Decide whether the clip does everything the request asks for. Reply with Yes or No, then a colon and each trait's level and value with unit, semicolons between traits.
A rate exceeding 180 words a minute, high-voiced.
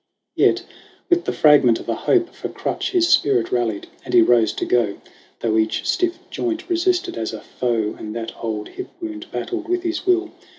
No: average, 195 wpm; medium, 150 Hz